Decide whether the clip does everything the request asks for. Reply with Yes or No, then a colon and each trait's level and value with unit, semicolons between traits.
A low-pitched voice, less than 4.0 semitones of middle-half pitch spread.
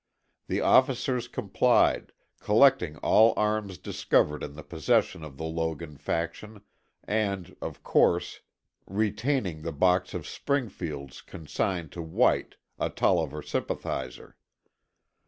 No: very low, 85 Hz; wide, 5.6 semitones